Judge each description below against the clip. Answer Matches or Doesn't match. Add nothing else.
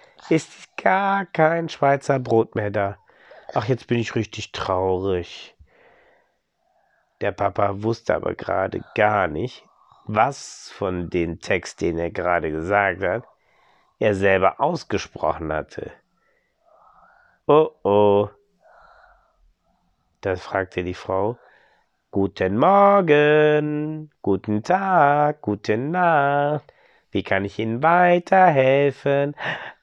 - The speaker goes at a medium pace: Doesn't match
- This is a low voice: Matches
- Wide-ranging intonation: Matches